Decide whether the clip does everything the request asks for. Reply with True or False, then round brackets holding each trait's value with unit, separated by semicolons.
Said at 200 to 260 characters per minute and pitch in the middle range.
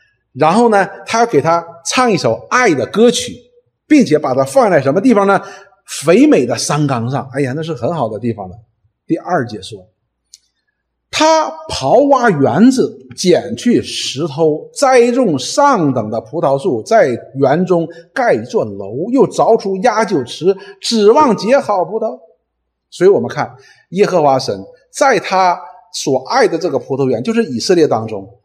True (225 characters per minute; 180 Hz)